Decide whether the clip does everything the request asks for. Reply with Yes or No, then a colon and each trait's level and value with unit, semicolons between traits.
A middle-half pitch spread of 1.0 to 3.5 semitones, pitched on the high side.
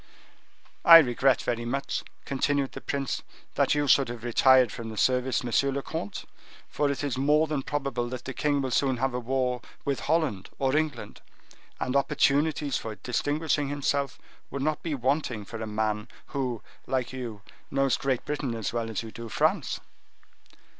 No: average, 2.9 semitones; low, 135 Hz